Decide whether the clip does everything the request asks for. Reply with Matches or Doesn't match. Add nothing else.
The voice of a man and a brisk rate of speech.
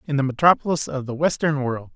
Matches